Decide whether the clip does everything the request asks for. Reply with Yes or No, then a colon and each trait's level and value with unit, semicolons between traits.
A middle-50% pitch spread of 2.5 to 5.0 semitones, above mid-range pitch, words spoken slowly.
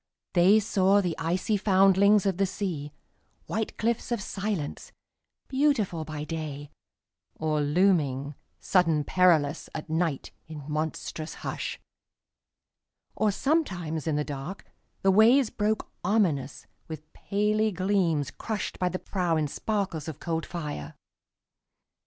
No: average, 4.7 semitones; medium, 175 Hz; slow, 110 wpm